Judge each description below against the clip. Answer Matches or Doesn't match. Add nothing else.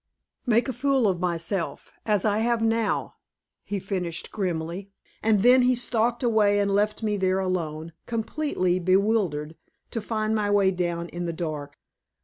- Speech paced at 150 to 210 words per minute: Matches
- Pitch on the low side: Doesn't match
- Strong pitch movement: Doesn't match